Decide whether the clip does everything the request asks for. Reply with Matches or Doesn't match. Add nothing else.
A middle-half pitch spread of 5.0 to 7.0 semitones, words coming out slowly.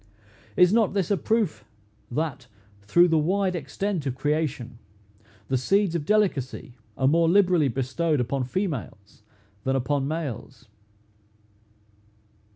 Matches